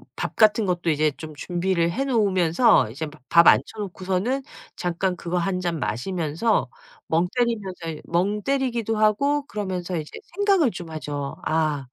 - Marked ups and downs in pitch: No, average, 4.8 semitones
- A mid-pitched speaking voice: Yes, medium, 180 Hz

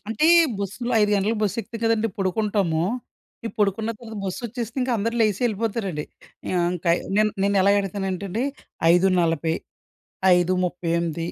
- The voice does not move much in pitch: No, average, 3.8 semitones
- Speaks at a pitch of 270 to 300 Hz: No, high, 200 Hz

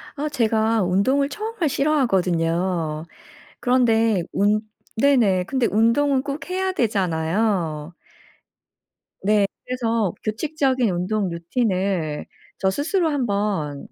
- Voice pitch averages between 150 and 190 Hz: No, high, 215 Hz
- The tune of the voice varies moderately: No, wide, 6.6 semitones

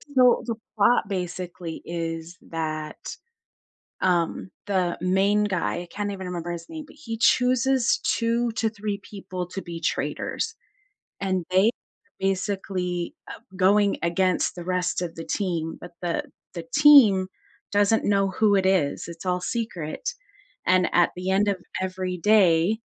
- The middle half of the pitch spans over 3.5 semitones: No, average, 2.9 semitones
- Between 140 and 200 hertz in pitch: Yes, high, 190 Hz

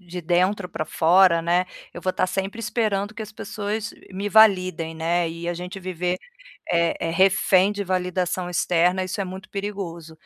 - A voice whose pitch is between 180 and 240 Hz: Yes, medium, 185 Hz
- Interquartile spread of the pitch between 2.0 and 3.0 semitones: Yes, narrow, 2.4 semitones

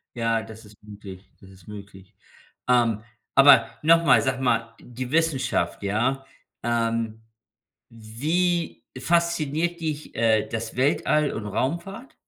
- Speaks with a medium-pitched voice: No, low, 120 Hz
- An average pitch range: No, wide, 5.7 semitones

